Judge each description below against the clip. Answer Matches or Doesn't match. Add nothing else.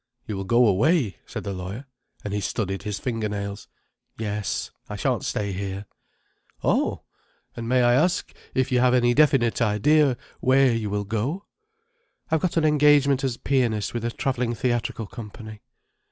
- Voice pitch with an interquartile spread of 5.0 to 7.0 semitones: Doesn't match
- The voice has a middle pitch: Doesn't match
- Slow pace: Doesn't match